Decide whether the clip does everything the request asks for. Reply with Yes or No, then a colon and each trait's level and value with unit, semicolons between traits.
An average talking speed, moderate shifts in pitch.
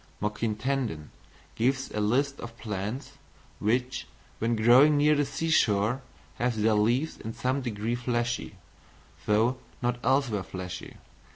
No: slow, 130 wpm; average, 3.7 semitones